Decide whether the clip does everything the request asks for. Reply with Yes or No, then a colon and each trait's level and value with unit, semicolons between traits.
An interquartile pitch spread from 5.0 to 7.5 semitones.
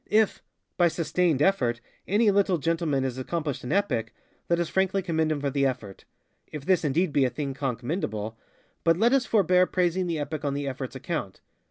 Yes: wide, 5.4 semitones